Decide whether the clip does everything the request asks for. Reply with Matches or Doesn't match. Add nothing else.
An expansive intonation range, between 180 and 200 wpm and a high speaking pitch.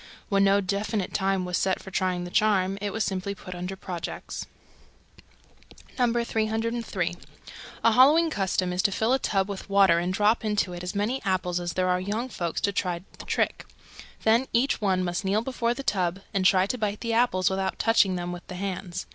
Doesn't match